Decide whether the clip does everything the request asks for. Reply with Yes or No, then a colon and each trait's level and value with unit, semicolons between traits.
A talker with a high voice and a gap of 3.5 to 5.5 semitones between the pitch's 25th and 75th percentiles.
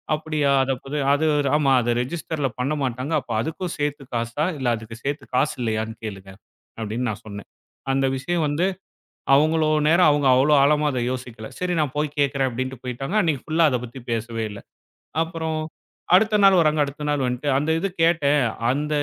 No: medium, 140 Hz; average, 3.8 semitones